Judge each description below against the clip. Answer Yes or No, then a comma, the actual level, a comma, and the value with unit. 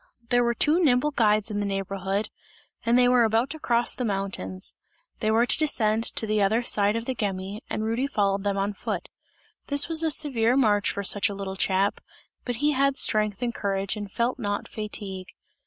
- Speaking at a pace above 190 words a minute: Yes, fast, 205 wpm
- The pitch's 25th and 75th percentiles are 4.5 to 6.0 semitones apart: No, average, 3.6 semitones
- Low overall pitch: No, high, 215 Hz